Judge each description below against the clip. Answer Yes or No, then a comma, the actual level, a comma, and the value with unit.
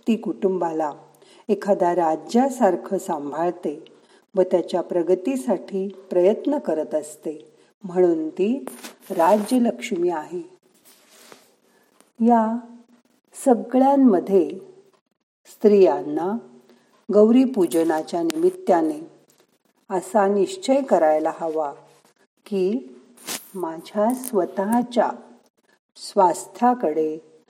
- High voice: Yes, high, 195 Hz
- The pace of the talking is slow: Yes, slow, 60 wpm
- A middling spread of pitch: No, wide, 6.1 semitones